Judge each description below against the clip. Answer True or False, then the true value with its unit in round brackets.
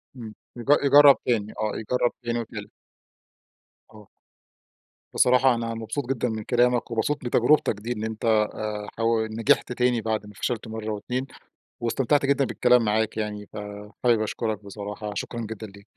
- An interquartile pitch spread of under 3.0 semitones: True (2.6 semitones)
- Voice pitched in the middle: False (115 Hz)